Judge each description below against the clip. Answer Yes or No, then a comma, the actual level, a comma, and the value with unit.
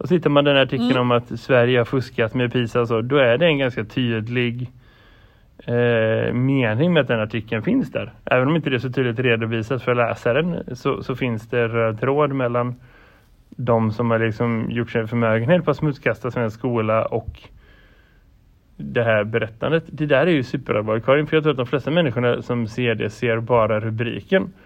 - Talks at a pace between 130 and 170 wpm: No, average, 190 wpm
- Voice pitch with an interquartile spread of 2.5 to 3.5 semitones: Yes, average, 2.8 semitones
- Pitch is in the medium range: No, low, 120 Hz